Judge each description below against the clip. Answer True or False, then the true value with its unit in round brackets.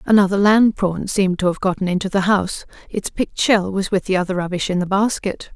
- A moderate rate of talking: False (225 wpm)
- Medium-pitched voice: False (195 Hz)